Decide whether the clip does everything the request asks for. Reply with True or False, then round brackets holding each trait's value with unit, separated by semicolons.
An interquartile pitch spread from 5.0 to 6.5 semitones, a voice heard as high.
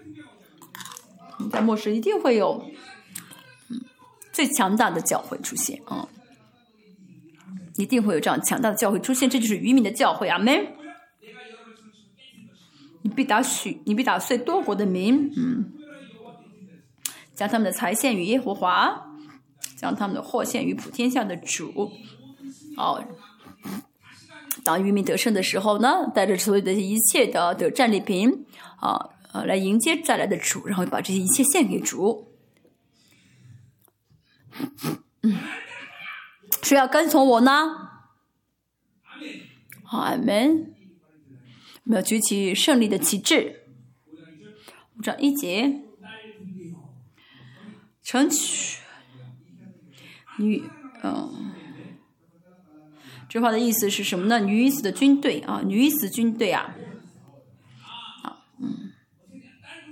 True (5.4 semitones; 220 Hz)